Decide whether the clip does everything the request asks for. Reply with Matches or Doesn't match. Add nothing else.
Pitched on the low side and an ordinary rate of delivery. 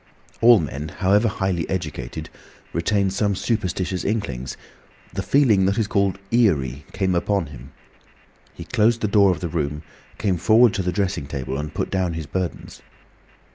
Matches